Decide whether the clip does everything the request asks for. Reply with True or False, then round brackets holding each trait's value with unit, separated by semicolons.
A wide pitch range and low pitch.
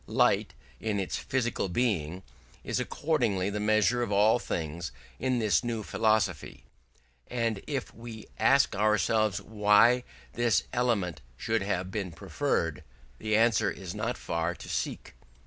False (3.3 semitones; 110 Hz)